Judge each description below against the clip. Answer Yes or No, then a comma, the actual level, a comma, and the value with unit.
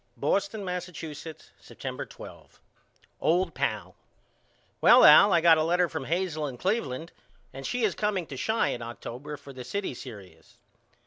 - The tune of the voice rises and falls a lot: Yes, wide, 5.9 semitones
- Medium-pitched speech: Yes, medium, 160 Hz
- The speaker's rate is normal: Yes, average, 150 wpm